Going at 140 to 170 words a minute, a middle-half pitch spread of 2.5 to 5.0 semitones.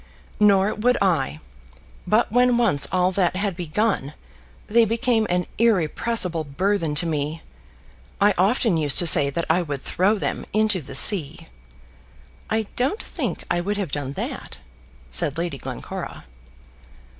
No: average, 145 wpm; wide, 5.4 semitones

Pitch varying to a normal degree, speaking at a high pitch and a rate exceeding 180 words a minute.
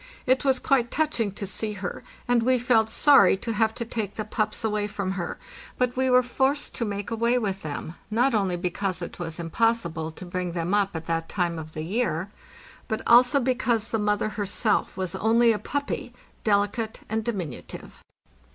Yes: average, 4.3 semitones; high, 215 Hz; average, 190 wpm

